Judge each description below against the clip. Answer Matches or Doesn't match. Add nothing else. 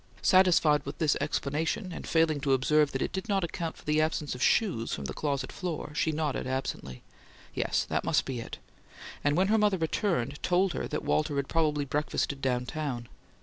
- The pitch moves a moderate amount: Matches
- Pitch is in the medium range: Matches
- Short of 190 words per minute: Doesn't match